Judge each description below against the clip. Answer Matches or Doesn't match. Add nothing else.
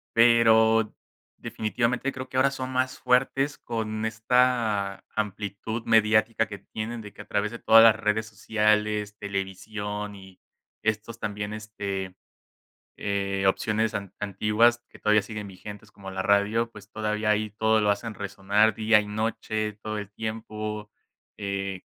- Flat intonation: Matches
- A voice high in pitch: Doesn't match